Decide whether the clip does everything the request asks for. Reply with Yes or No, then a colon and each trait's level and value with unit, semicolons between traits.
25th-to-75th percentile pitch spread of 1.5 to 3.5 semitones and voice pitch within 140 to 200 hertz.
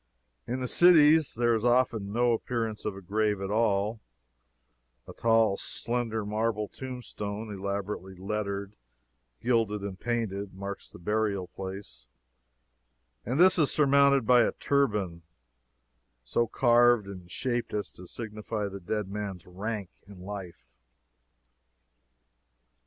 No: average, 3.2 semitones; low, 105 Hz